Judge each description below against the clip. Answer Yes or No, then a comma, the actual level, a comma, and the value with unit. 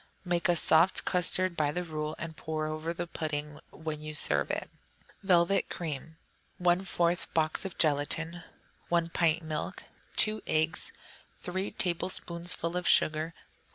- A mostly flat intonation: Yes, narrow, 2.1 semitones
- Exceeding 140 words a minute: No, slow, 135 wpm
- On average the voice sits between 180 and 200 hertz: No, medium, 165 Hz